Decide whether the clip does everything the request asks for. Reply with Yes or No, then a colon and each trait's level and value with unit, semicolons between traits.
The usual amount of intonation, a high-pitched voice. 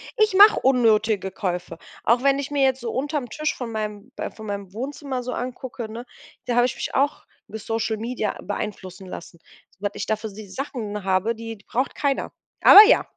Yes: average, 4.0 semitones; high, 230 Hz